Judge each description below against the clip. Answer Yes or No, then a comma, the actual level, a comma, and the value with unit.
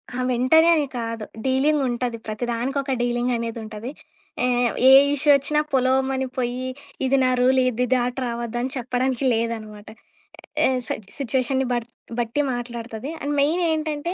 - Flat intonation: Yes, narrow, 2.3 semitones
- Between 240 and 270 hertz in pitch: Yes, very high, 250 Hz